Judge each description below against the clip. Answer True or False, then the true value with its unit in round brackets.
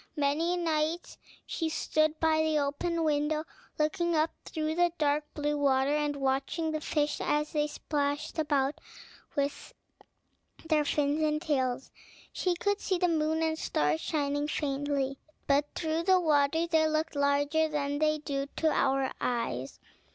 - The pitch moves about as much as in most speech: False (2.0 semitones)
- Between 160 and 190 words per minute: False (150 wpm)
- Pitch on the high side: True (300 Hz)